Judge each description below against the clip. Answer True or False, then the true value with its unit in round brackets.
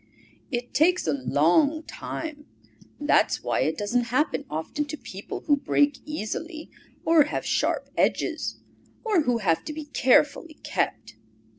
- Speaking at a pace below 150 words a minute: True (140 wpm)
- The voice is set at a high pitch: True (290 Hz)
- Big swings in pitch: False (4.8 semitones)